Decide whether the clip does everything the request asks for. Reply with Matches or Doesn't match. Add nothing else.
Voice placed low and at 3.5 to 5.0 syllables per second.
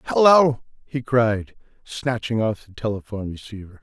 Matches